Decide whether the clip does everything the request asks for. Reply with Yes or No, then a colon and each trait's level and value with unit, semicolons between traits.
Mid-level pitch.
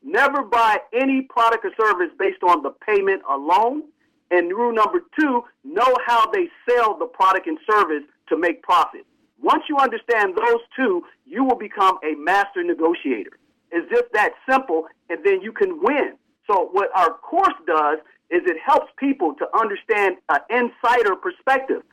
No: very high, 270 Hz